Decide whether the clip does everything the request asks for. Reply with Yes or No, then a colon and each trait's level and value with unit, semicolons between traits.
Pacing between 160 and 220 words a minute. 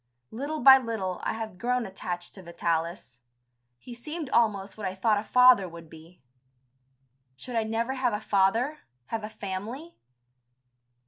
No: average, 150 wpm